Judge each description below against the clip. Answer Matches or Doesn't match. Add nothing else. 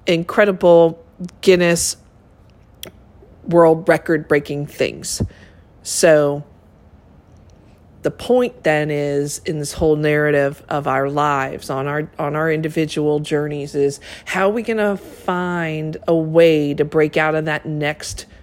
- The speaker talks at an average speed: Doesn't match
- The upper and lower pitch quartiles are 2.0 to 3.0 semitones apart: Doesn't match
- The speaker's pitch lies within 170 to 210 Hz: Doesn't match